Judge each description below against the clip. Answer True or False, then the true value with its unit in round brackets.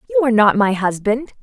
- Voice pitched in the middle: False (210 Hz)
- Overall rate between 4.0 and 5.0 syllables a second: False (6.3 syllables/s)